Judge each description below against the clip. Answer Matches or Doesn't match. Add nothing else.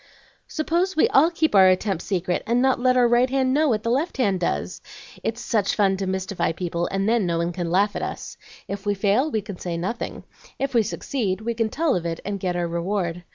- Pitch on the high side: Matches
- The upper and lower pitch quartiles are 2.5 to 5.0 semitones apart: Doesn't match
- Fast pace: Matches